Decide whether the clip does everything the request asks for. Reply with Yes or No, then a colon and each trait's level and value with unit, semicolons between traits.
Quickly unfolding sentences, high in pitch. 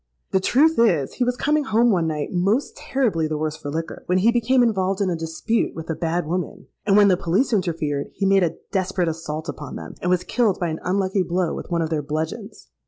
No: fast, 235 wpm; medium, 180 Hz